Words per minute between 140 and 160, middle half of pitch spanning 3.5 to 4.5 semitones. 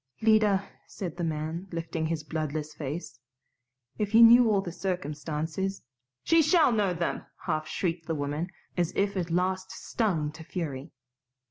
Yes: average, 155 wpm; average, 4.1 semitones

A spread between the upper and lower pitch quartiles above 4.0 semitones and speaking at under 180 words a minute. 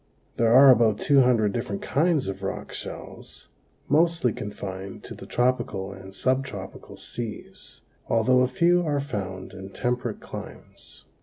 Yes: average, 5.3 semitones; average, 140 wpm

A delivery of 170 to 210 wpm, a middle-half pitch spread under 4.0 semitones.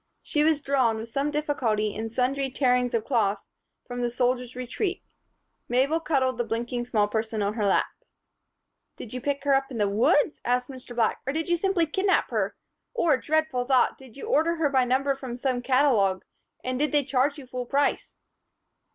Yes: average, 190 wpm; average, 3.1 semitones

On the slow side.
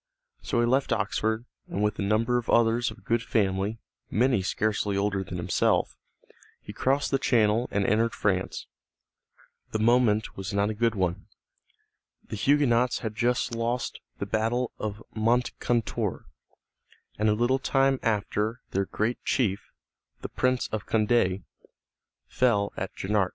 No: average, 145 wpm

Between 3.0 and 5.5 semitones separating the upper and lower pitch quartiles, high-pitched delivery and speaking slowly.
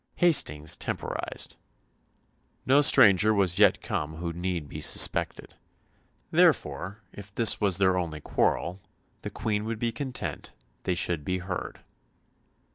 No: average, 3.8 semitones; very low, 95 Hz; slow, 125 wpm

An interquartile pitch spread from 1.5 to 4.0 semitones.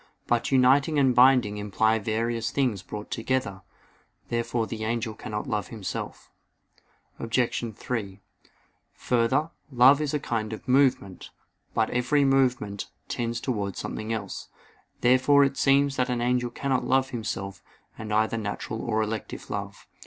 Yes: average, 3.2 semitones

